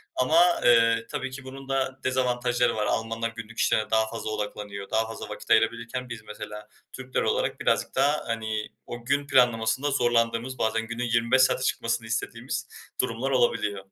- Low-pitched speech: Yes, low, 115 Hz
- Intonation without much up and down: Yes, narrow, 2.3 semitones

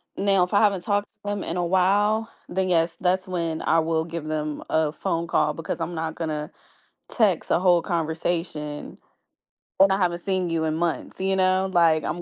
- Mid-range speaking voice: Yes, medium, 175 Hz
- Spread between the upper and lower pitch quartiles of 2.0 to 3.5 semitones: Yes, average, 2.8 semitones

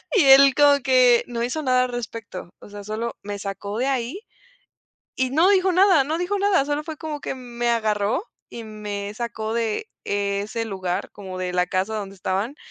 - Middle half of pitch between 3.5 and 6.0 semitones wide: Yes, average, 5.3 semitones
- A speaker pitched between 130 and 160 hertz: No, high, 235 Hz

